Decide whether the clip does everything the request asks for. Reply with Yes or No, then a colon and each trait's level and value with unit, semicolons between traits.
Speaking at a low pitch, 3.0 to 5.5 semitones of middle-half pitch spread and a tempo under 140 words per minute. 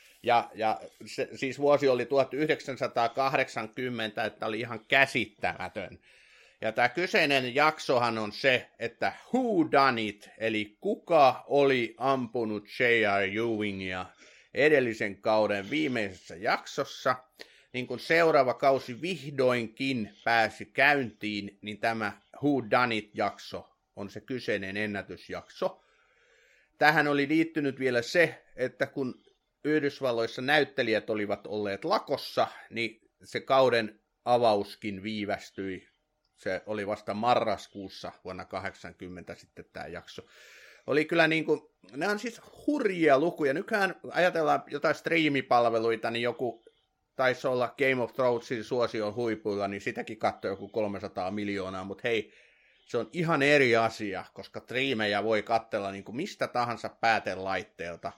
Yes: low, 120 Hz; average, 4.7 semitones; average, 115 wpm